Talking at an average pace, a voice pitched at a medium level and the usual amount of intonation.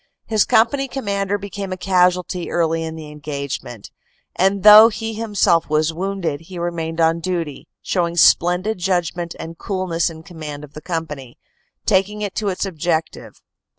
Yes: average, 160 wpm; medium, 175 Hz; average, 3.5 semitones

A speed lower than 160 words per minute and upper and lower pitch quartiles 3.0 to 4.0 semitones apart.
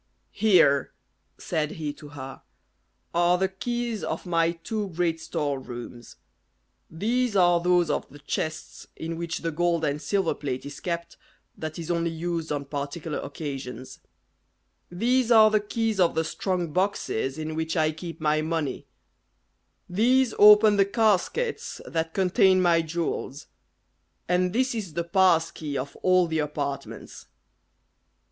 Yes: average, 145 wpm; average, 3.7 semitones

